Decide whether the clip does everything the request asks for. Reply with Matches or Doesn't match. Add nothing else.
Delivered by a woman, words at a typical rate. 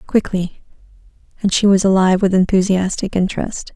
Doesn't match